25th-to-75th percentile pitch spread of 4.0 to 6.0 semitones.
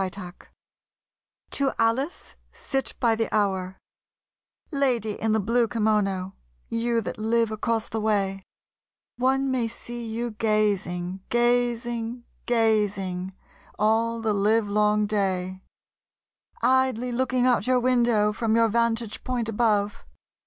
No: narrow, 2.4 semitones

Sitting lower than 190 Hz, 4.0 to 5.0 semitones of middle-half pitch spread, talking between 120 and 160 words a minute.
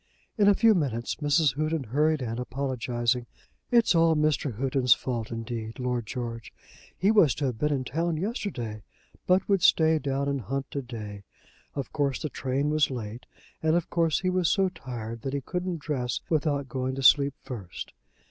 No: medium, 140 Hz; average, 4.5 semitones; average, 180 wpm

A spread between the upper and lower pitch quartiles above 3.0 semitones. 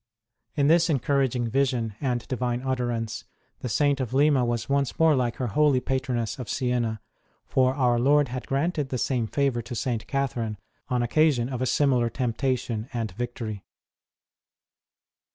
No: narrow, 2.6 semitones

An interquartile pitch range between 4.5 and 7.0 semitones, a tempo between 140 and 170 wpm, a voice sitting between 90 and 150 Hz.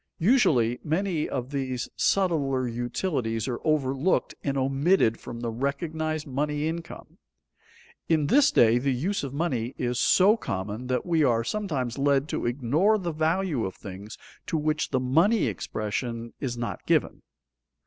Yes: average, 4.9 semitones; average, 150 wpm; medium, 140 Hz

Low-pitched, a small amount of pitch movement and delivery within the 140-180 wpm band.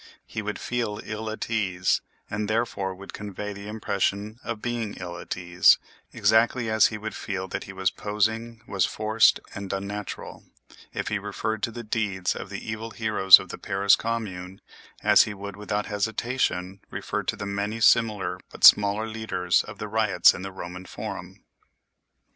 Yes: low, 105 Hz; narrow, 2.3 semitones; average, 170 wpm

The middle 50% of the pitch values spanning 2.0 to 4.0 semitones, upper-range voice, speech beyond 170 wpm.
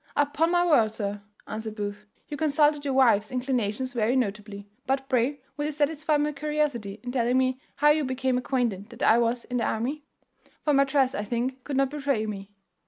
No: average, 4.6 semitones; very high, 260 Hz; average, 195 wpm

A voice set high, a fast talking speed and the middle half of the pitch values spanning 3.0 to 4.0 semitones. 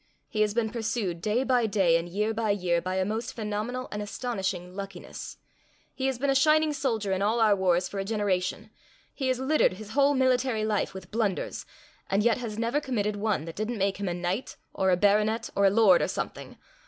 Yes: high, 210 Hz; fast, 215 wpm; average, 3.7 semitones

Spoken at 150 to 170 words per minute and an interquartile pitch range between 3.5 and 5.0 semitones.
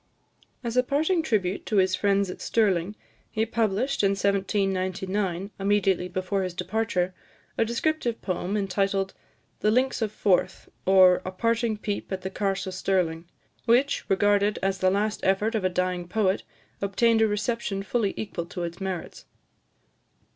No: average, 155 wpm; average, 2.8 semitones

